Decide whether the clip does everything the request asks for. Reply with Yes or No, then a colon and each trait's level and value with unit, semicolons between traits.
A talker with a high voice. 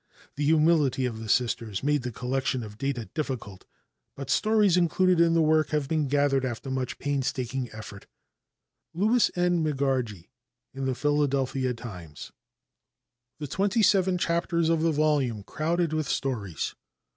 No: medium, 140 Hz